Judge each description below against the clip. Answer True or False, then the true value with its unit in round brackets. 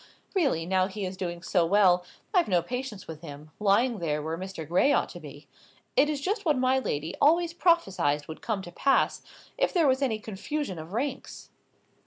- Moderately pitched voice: False (195 Hz)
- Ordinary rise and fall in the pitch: False (8.1 semitones)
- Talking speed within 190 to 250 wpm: True (195 wpm)